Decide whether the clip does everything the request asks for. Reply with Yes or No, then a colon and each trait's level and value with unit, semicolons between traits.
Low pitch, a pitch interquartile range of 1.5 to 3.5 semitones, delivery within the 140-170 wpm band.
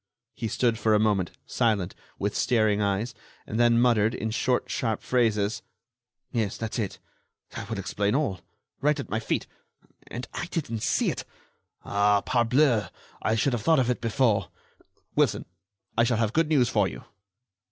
Yes: low, 115 Hz; average, 2.9 semitones; average, 165 wpm